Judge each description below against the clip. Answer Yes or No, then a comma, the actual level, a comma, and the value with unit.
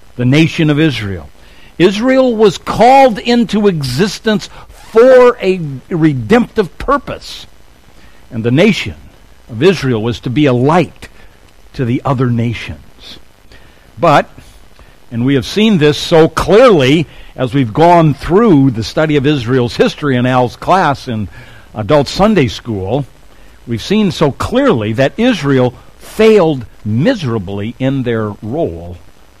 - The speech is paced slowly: Yes, slow, 125 wpm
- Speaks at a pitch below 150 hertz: Yes, low, 135 Hz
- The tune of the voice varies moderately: No, wide, 7.4 semitones